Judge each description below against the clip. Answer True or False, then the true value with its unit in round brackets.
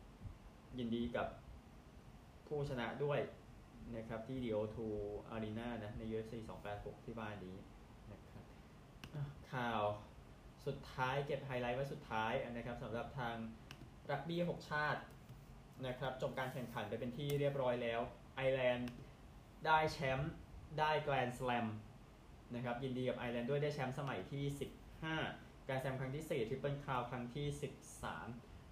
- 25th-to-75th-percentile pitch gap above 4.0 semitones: False (3.6 semitones)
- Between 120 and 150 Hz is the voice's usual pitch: True (125 Hz)